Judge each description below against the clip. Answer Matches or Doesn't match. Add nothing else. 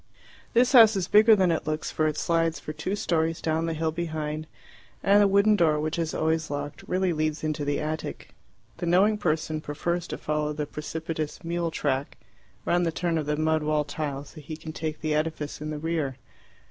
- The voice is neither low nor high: Matches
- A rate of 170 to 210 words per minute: Matches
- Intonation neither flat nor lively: Doesn't match